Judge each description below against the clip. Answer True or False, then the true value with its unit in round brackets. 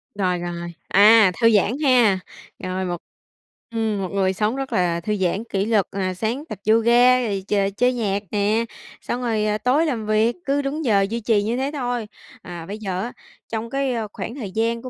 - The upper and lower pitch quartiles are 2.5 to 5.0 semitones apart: True (3.7 semitones)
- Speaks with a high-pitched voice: True (220 Hz)